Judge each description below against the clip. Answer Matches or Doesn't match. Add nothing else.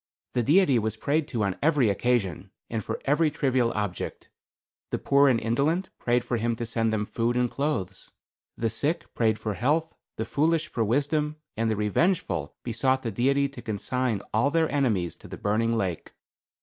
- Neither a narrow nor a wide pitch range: Matches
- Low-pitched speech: Matches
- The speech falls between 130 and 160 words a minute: Doesn't match